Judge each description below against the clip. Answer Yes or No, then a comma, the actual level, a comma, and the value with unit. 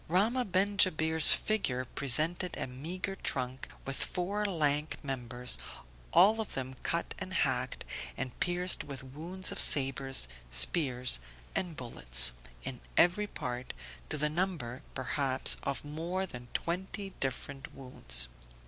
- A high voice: No, medium, 145 Hz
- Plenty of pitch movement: Yes, wide, 6.1 semitones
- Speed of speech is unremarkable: No, slow, 130 wpm